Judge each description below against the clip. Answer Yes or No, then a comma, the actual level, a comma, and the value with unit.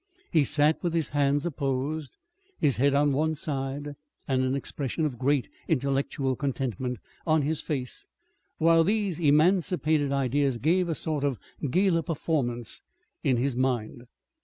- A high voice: No, medium, 145 Hz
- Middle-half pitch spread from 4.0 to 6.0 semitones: No, average, 3.1 semitones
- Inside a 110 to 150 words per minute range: Yes, average, 140 wpm